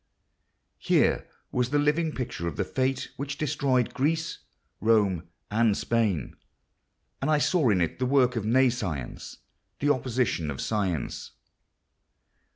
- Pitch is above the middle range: No, low, 125 Hz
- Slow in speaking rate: Yes, slow, 125 wpm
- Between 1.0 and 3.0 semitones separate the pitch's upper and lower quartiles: No, wide, 5.4 semitones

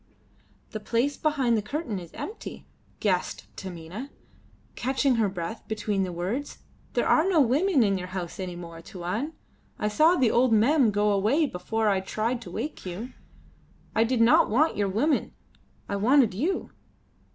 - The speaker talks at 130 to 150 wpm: No, average, 165 wpm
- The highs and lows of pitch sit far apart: Yes, wide, 6.0 semitones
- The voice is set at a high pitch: Yes, high, 220 Hz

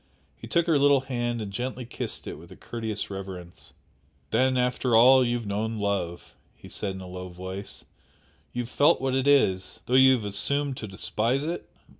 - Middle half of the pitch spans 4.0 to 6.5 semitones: Yes, average, 4.9 semitones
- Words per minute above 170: Yes, average, 190 wpm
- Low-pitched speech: Yes, low, 120 Hz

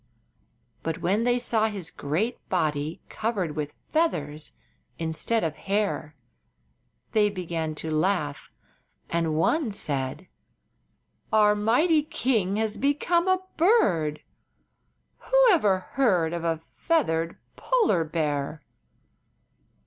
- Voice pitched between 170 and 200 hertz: Yes, high, 190 Hz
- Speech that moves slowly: Yes, slow, 110 wpm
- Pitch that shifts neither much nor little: No, wide, 6.9 semitones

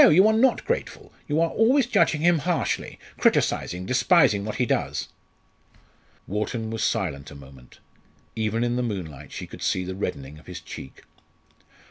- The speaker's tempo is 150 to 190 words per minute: Yes, average, 160 wpm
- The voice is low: Yes, low, 110 Hz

